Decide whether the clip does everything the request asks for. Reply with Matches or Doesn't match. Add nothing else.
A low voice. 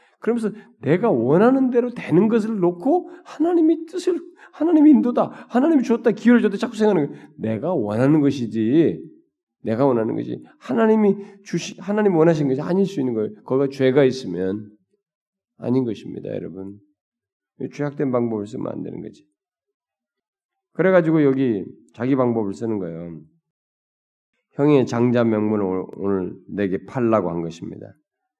Doesn't match